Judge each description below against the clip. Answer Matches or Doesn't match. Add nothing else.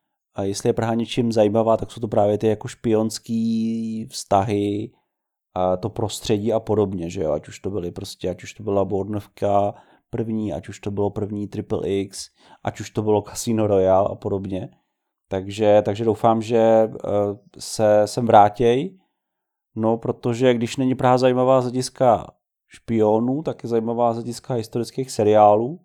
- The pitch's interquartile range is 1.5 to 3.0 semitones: Matches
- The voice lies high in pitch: Doesn't match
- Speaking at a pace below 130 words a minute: Doesn't match